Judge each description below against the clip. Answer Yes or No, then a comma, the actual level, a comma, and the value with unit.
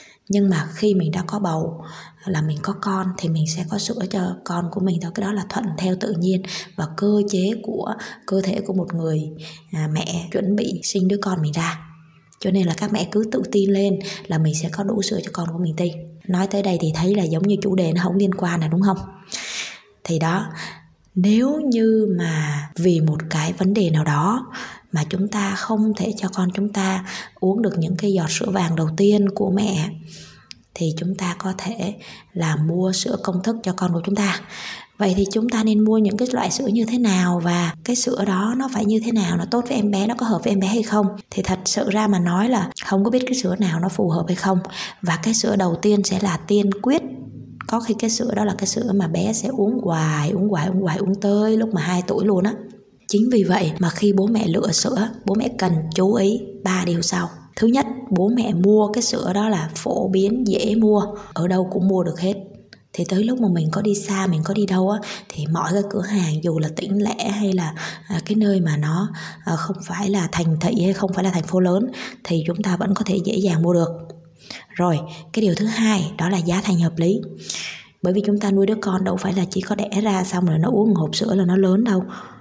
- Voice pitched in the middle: No, high, 195 Hz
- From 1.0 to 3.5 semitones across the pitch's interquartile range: Yes, average, 2.9 semitones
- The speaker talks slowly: No, average, 245 wpm